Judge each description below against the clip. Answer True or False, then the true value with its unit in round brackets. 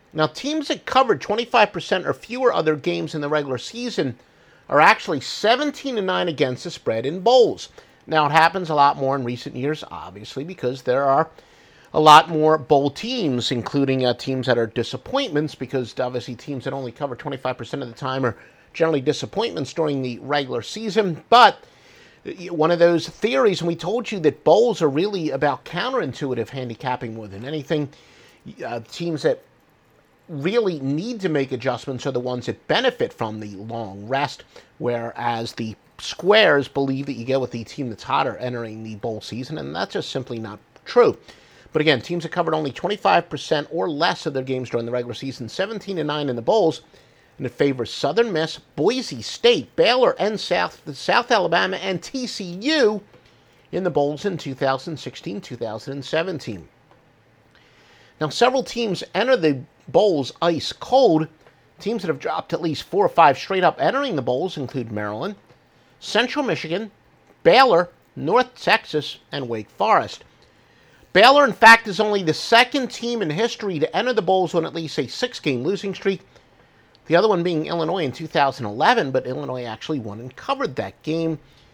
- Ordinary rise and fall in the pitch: False (6.7 semitones)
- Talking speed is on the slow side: False (170 wpm)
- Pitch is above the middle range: False (150 Hz)